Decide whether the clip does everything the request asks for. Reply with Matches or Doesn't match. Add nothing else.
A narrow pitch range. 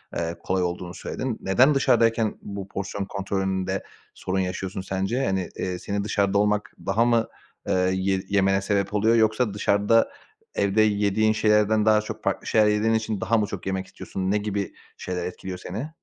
Matches